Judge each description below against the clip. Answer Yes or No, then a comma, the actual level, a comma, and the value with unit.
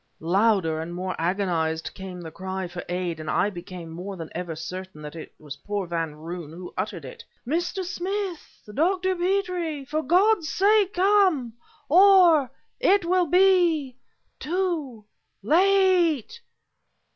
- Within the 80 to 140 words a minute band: Yes, slow, 135 wpm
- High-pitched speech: Yes, very high, 255 Hz